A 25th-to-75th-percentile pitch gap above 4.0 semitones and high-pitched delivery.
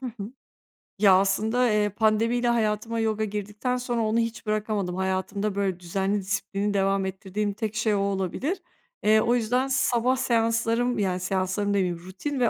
No: average, 2.8 semitones; high, 210 Hz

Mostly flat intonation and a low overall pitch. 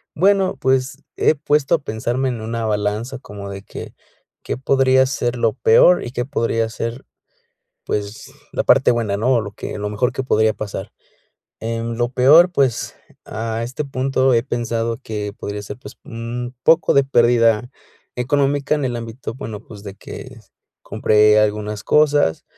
No: average, 3.5 semitones; low, 120 Hz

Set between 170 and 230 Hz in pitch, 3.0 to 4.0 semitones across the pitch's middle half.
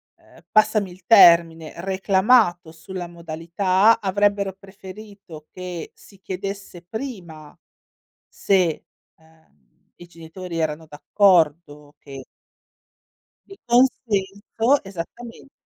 Yes: medium, 185 Hz; average, 3.6 semitones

